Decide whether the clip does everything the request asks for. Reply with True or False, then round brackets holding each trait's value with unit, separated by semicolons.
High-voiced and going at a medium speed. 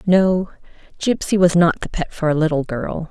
False (170 Hz; 195 wpm)